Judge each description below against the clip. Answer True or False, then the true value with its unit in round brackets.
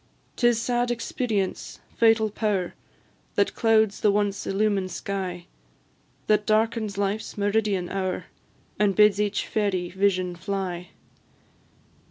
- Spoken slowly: True (110 wpm)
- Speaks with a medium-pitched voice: False (205 Hz)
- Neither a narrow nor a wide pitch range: False (2.2 semitones)